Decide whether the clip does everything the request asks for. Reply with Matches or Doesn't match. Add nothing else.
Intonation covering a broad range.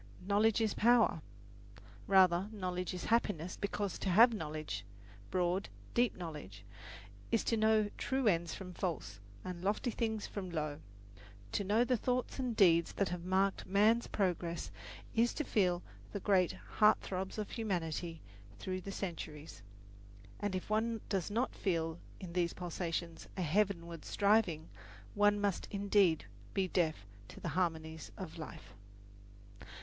Doesn't match